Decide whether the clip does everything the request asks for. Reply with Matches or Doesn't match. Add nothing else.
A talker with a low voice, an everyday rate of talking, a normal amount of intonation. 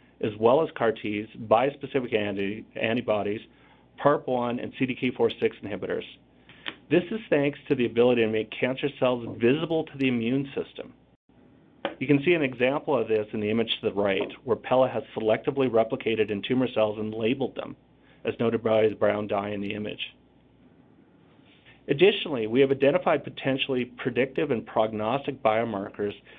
Matches